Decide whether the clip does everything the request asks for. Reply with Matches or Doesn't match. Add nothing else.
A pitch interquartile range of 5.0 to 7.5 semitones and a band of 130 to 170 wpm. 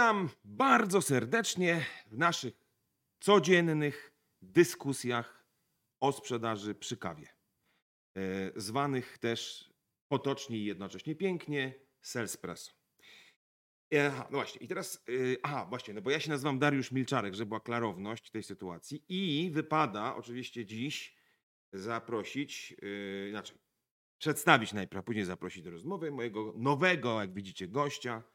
Doesn't match